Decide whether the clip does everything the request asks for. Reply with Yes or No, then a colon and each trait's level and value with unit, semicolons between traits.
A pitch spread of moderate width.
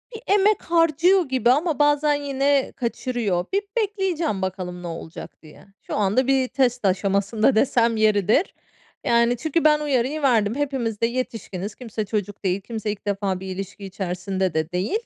No: wide, 6.6 semitones